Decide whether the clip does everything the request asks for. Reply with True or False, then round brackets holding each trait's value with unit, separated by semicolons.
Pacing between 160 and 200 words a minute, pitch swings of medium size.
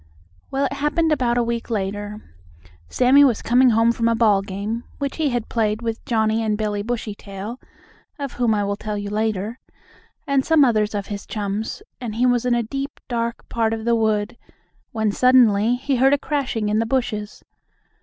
True (190 wpm; 3.0 semitones)